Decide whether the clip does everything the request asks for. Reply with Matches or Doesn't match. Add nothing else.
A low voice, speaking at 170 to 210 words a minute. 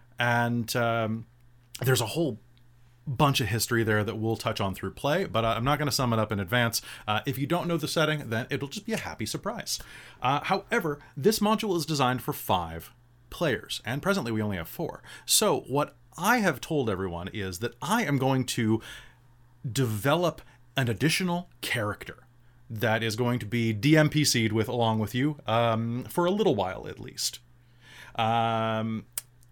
Matches